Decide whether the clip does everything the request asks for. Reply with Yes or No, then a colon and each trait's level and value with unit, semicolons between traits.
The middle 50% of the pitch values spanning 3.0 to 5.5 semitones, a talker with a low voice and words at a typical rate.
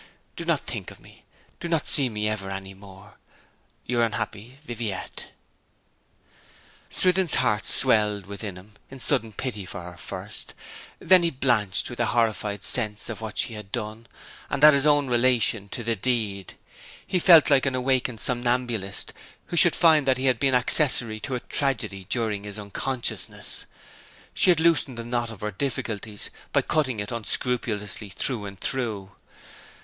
Yes: average, 4.1 semitones; low, 115 Hz; average, 165 wpm